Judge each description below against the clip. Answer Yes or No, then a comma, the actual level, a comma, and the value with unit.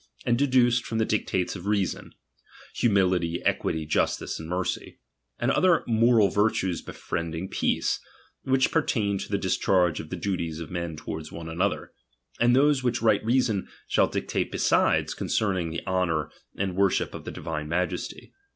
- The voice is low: Yes, very low, 95 Hz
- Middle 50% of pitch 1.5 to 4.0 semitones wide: No, average, 5.3 semitones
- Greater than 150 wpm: Yes, average, 160 wpm